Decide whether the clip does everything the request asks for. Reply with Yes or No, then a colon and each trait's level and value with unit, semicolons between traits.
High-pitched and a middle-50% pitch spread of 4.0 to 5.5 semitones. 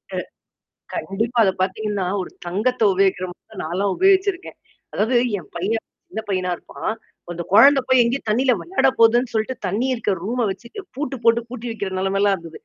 Yes: high, 220 Hz; average, 4.5 semitones